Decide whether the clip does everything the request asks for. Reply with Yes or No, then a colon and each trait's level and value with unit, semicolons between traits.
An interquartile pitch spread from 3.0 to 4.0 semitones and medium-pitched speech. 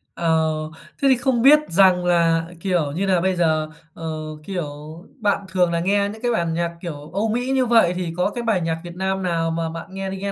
Yes: average, 3.3 semitones; medium, 180 Hz